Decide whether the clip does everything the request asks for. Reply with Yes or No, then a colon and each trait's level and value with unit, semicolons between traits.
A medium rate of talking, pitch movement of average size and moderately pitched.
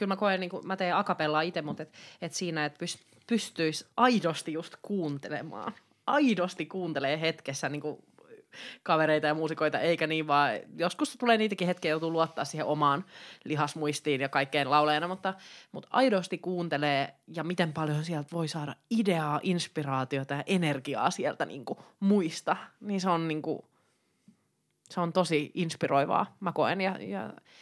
No: fast, 160 wpm; average, 3.7 semitones; medium, 165 Hz